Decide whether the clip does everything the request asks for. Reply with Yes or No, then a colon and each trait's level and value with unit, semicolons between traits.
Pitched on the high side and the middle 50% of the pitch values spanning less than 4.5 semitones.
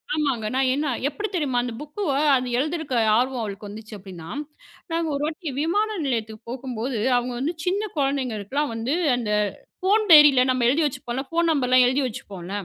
No: very high, 265 Hz; average, 4.8 semitones